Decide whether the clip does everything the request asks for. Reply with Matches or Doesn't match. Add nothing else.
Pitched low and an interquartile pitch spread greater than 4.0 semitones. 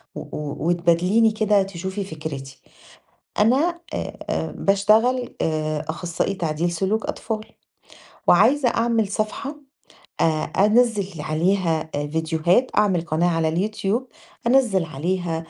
Doesn't match